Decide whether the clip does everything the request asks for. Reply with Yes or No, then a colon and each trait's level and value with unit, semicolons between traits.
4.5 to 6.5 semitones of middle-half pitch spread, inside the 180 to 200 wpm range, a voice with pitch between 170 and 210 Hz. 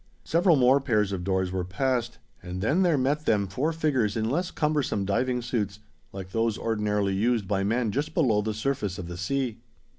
No: wide, 5.5 semitones; average, 190 wpm; low, 115 Hz